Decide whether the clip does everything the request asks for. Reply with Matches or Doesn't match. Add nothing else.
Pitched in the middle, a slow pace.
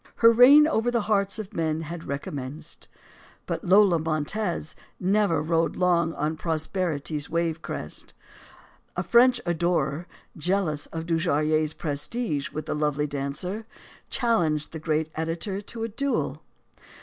Matches